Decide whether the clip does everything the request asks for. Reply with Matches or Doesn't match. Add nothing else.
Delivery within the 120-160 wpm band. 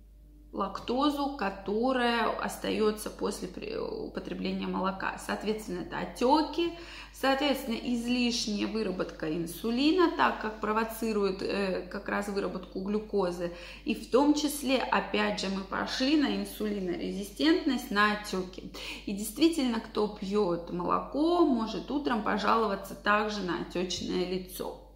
Doesn't match